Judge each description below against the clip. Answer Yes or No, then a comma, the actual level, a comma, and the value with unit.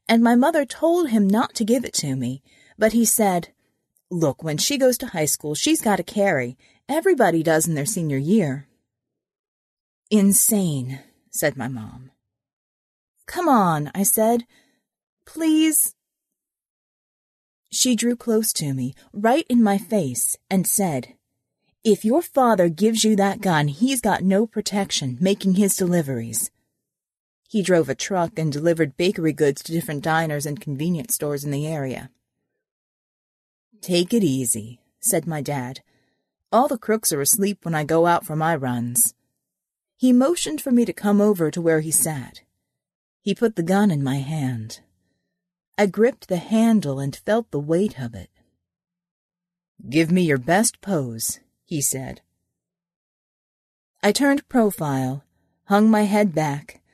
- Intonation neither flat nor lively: No, wide, 7.2 semitones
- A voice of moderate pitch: Yes, medium, 175 Hz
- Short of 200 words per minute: Yes, average, 150 wpm